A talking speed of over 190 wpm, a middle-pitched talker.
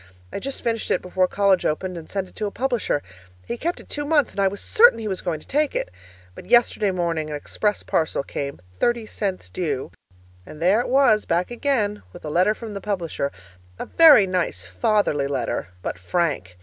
No: fast, 205 wpm; high, 195 Hz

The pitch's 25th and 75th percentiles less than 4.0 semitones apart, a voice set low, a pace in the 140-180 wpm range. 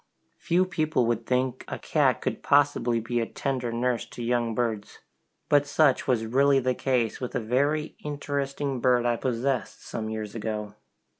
Yes: average, 3.2 semitones; low, 125 Hz; average, 165 wpm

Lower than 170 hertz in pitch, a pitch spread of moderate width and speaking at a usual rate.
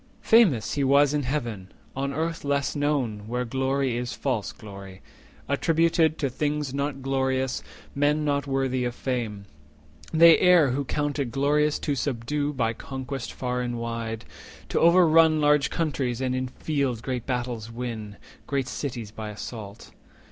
Yes: low, 135 Hz; average, 3.6 semitones; average, 155 wpm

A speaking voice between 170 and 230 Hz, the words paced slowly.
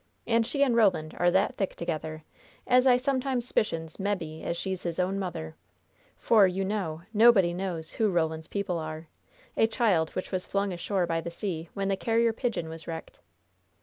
No: medium, 185 Hz; average, 180 wpm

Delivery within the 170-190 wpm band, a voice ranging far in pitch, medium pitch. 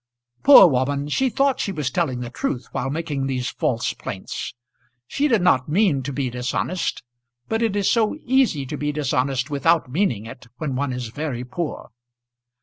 Yes: average, 175 wpm; wide, 6.2 semitones; medium, 145 Hz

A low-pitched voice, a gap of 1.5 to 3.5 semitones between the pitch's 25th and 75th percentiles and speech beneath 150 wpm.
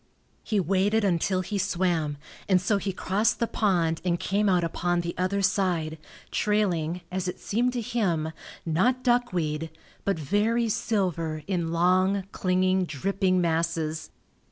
No: medium, 185 Hz; average, 3.2 semitones; average, 140 wpm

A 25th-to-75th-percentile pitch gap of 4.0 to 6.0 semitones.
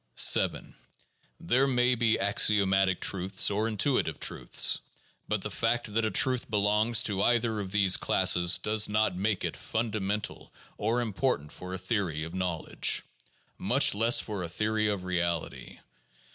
No: average, 3.2 semitones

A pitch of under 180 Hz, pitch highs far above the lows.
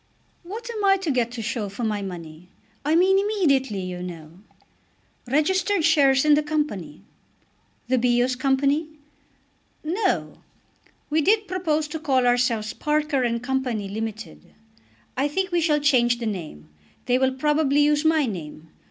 No: very high, 265 Hz; wide, 5.7 semitones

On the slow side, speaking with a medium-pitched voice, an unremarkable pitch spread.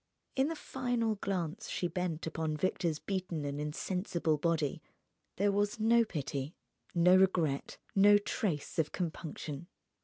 Yes: slow, 130 wpm; medium, 175 Hz; average, 4.6 semitones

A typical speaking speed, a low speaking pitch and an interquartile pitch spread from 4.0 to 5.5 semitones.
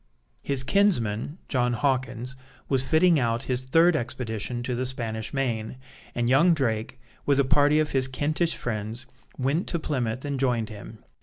No: average, 160 wpm; low, 130 Hz; average, 3.4 semitones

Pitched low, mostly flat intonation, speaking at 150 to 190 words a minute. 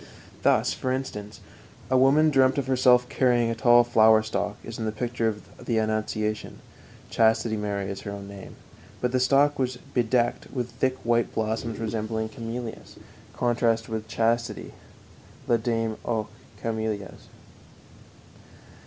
No: low, 115 Hz; narrow, 2.1 semitones; average, 140 wpm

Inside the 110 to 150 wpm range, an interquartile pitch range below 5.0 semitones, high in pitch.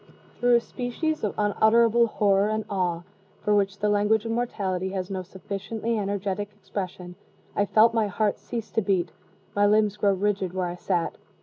No: average, 175 wpm; narrow, 2.4 semitones; high, 205 Hz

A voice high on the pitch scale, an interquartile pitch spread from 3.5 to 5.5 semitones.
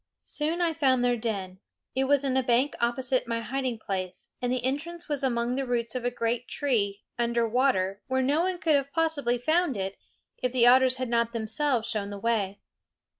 No: high, 245 Hz; average, 3.0 semitones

